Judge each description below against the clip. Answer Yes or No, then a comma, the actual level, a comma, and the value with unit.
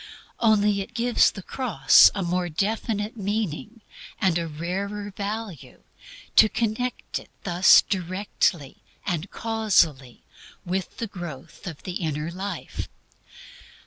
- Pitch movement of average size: Yes, average, 3.9 semitones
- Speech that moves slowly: Yes, slow, 120 wpm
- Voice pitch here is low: No, high, 195 Hz